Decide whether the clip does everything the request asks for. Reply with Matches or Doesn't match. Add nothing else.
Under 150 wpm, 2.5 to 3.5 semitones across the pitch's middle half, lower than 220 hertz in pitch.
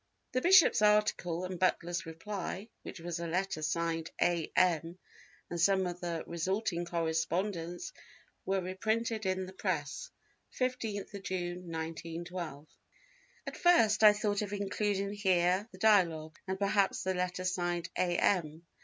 Matches